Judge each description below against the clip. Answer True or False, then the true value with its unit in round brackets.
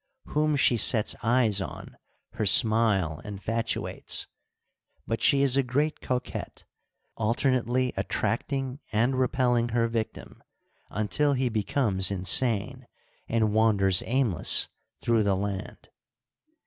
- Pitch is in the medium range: False (115 Hz)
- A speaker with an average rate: False (110 wpm)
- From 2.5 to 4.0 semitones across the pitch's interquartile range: True (3.5 semitones)